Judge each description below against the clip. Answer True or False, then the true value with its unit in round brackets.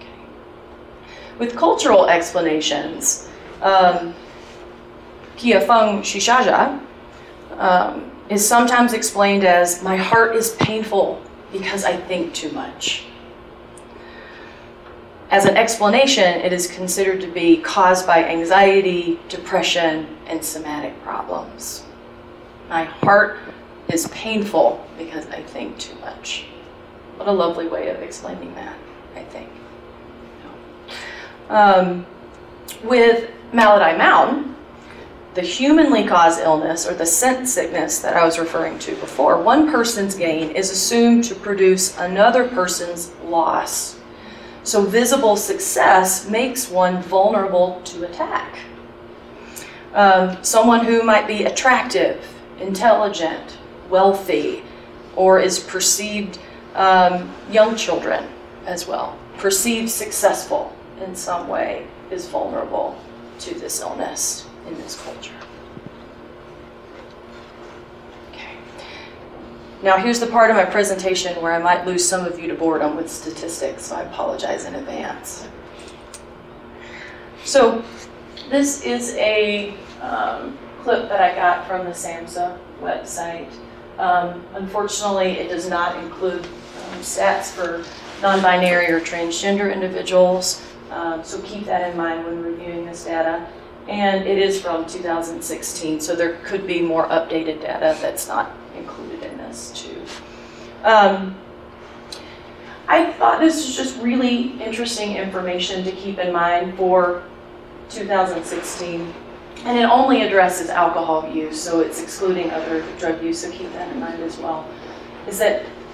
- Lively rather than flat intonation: False (3.5 semitones)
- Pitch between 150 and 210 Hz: True (185 Hz)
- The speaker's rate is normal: False (120 wpm)